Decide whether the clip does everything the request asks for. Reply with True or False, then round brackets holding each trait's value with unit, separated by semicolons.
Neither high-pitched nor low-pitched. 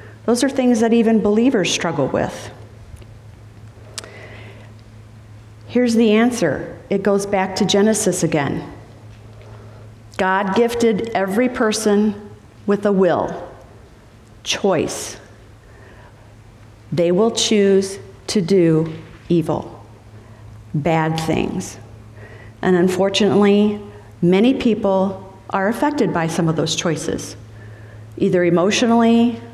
True (160 Hz)